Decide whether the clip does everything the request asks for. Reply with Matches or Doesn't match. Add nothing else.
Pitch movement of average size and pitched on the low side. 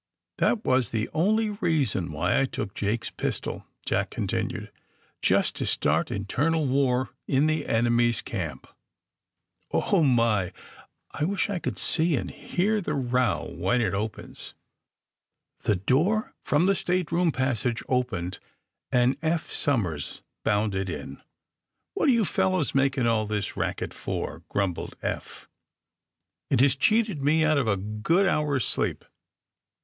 Doesn't match